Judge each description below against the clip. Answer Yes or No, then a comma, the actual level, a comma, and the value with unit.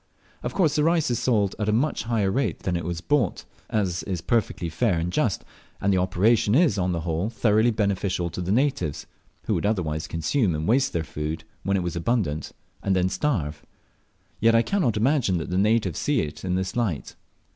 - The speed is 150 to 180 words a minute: No, fast, 205 wpm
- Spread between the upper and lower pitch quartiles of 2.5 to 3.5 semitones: No, average, 5.1 semitones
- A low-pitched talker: Yes, low, 100 Hz